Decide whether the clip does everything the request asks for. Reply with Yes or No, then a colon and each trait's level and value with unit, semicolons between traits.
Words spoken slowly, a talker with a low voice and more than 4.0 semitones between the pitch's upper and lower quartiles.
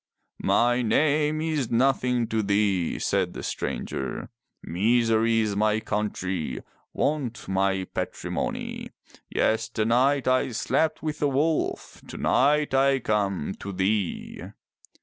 Yes: slow, 110 wpm; low, 115 Hz; average, 5.1 semitones